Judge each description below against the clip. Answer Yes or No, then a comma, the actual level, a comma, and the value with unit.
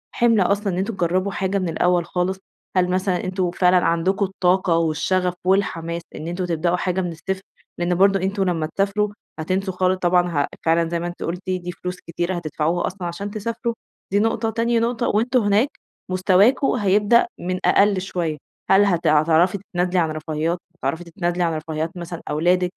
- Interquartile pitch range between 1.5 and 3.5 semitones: Yes, narrow, 2.4 semitones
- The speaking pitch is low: No, medium, 180 Hz